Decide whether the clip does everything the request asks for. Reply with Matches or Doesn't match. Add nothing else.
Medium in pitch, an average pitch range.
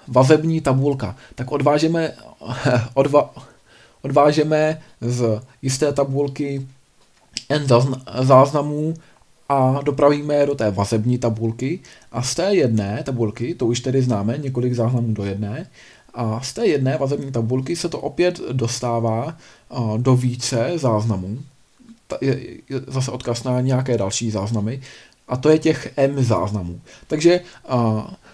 Doesn't match